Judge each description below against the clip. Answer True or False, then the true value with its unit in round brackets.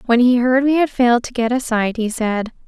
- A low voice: False (240 Hz)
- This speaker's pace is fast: True (270 wpm)